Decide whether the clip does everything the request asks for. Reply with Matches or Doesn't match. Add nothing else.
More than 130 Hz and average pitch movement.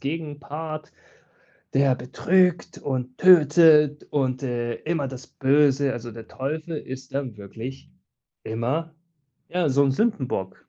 Matches